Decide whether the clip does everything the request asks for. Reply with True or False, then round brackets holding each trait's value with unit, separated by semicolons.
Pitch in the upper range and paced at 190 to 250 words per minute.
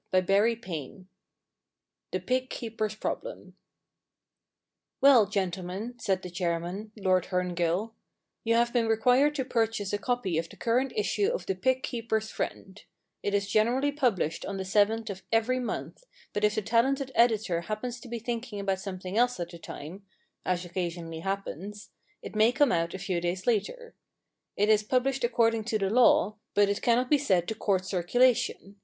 False (215 Hz; 175 wpm)